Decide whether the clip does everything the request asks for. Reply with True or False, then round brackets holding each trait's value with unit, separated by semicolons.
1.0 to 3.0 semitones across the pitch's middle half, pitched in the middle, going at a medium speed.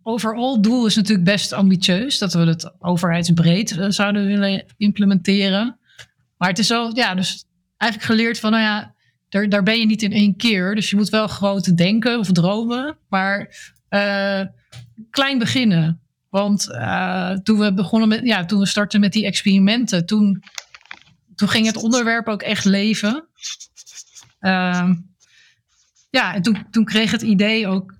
False (2.4 semitones; 205 Hz; 160 wpm)